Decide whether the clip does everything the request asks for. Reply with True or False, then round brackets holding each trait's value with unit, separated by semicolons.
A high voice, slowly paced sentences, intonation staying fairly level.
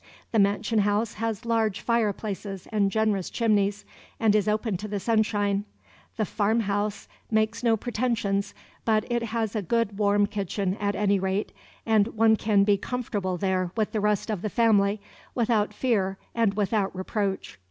False (210 Hz; 165 wpm; 1.9 semitones)